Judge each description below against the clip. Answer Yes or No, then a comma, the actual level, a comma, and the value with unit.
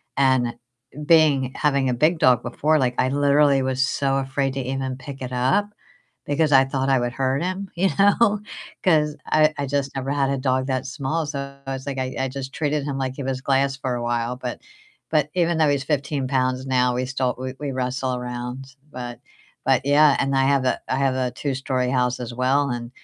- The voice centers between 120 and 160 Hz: Yes, low, 135 Hz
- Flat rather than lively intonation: Yes, narrow, 1.8 semitones